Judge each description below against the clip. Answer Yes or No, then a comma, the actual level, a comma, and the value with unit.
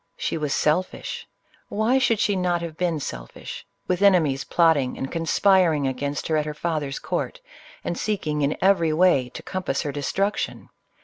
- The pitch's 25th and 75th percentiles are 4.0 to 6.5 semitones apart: Yes, average, 4.3 semitones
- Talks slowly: No, average, 185 wpm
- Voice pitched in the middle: Yes, medium, 165 Hz